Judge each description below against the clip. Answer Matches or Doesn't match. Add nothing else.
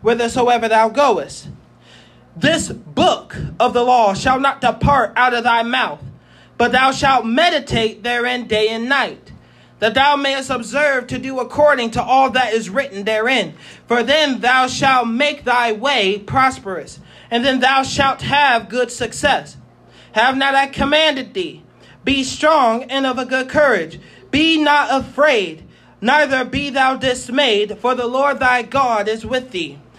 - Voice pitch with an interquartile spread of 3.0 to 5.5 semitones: Doesn't match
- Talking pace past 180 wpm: Doesn't match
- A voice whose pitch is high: Matches